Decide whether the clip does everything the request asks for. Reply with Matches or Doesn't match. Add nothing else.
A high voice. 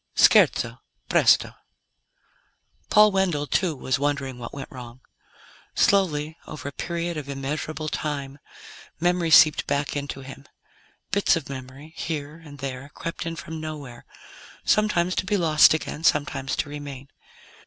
Doesn't match